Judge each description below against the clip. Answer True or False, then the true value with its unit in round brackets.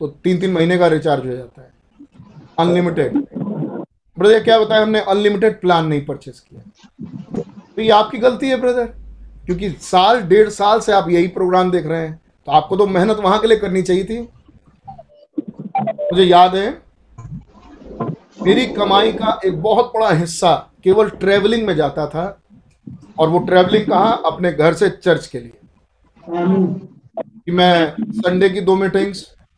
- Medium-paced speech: True (160 wpm)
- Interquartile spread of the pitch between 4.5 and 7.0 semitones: False (3.9 semitones)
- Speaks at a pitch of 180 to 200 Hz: True (190 Hz)